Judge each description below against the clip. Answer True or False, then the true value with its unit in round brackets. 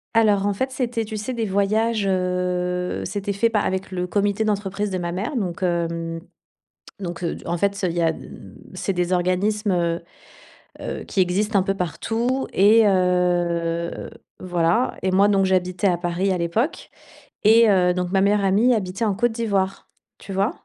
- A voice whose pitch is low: False (190 Hz)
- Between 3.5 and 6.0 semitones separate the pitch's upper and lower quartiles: False (2.7 semitones)